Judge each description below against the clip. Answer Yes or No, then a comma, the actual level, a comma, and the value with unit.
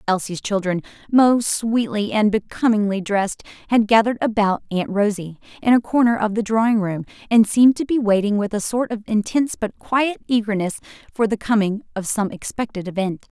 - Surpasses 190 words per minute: No, average, 175 wpm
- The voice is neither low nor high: No, high, 215 Hz